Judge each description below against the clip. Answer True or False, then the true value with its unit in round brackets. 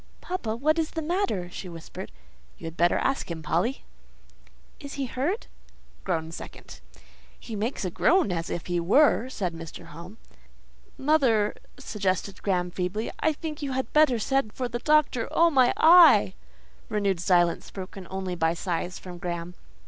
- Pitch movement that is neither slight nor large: False (7.9 semitones)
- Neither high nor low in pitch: False (205 Hz)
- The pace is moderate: True (160 wpm)